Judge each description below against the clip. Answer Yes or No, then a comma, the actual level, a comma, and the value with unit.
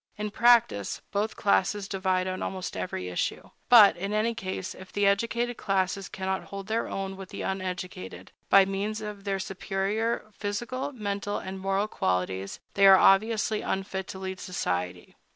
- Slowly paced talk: No, average, 160 wpm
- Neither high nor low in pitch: No, high, 195 Hz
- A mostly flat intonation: Yes, narrow, 1.9 semitones